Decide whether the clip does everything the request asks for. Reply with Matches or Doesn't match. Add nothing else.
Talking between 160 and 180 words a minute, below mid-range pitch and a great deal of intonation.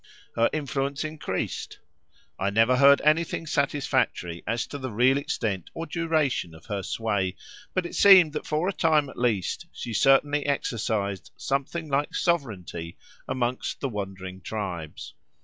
Doesn't match